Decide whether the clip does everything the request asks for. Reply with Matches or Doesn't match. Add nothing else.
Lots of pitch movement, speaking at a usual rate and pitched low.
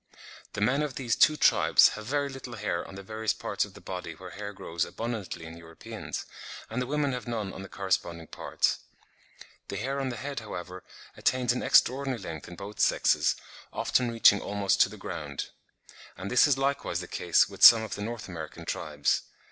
Matches